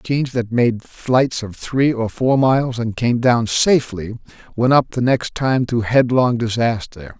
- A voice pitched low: Yes, low, 120 Hz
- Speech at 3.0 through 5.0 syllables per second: Yes, 4.4 syllables/s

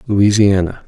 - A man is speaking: Yes, male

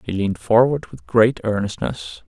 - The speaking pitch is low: Yes, low, 105 Hz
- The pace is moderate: Yes, average, 155 wpm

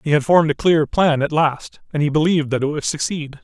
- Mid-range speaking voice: Yes, medium, 150 Hz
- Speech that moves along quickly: Yes, fast, 260 wpm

